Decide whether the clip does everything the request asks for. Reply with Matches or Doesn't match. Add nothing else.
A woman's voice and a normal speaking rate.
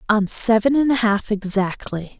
Matches